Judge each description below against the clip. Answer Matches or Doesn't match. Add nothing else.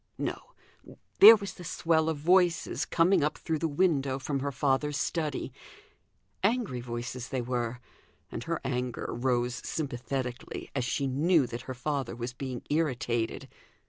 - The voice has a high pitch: Doesn't match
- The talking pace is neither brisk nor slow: Matches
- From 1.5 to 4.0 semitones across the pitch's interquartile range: Doesn't match